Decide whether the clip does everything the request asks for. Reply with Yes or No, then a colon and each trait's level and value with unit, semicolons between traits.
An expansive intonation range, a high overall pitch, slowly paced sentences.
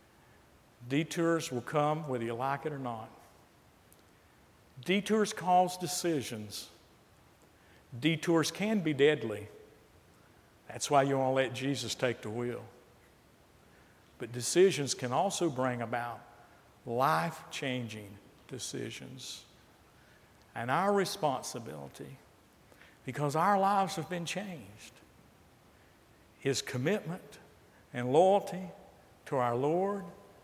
No: wide, 6.1 semitones; low, 135 Hz; slow, 100 wpm